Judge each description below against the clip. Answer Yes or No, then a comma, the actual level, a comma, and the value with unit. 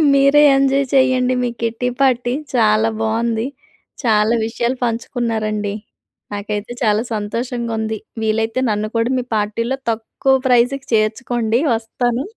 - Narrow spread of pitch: Yes, narrow, 2.3 semitones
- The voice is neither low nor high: No, high, 230 Hz